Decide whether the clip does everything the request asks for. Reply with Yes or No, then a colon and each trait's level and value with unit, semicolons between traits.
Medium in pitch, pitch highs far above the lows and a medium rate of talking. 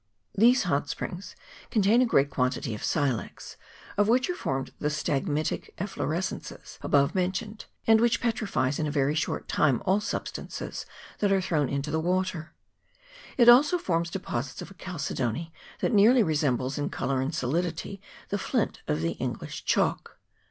Yes: medium, 165 Hz; wide, 6.2 semitones; average, 160 wpm